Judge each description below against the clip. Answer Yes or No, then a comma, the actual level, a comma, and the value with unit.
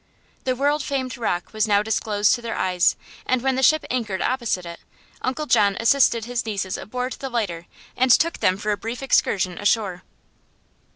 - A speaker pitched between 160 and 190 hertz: No, high, 230 Hz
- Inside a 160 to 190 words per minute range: Yes, average, 180 wpm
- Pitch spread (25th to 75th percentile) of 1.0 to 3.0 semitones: No, average, 4.2 semitones